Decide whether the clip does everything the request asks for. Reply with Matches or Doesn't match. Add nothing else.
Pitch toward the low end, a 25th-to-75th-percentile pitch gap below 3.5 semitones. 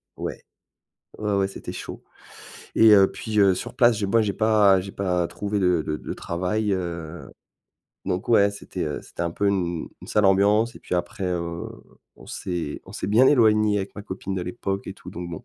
Matches